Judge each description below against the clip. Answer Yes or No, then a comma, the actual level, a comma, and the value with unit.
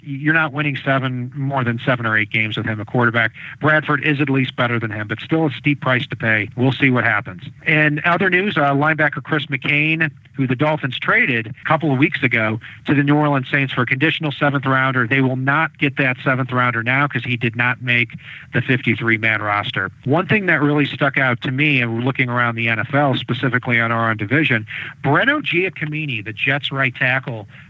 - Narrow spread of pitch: No, average, 3.3 semitones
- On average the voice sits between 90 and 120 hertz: No, low, 135 Hz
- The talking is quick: Yes, fast, 215 wpm